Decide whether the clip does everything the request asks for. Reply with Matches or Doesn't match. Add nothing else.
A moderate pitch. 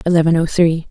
Matches